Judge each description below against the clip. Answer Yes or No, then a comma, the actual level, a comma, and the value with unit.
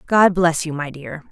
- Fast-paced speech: Yes, fast, 230 wpm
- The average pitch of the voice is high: No, medium, 165 Hz